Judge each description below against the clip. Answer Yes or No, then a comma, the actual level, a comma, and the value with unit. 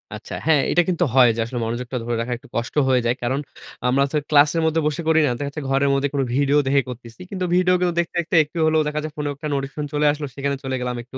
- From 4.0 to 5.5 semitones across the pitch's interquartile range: No, average, 3.3 semitones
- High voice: No, medium, 140 Hz